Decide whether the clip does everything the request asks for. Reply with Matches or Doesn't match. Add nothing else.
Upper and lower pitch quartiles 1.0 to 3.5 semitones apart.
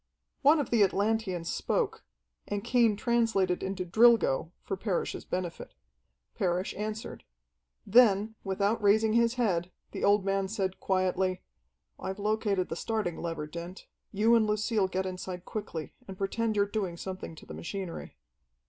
Matches